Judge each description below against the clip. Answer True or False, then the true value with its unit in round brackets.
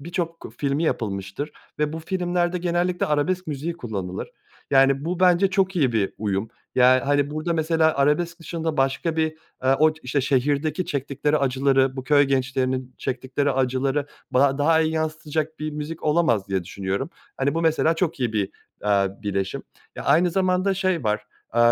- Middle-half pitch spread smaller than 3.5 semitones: False (4.0 semitones)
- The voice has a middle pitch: True (145 Hz)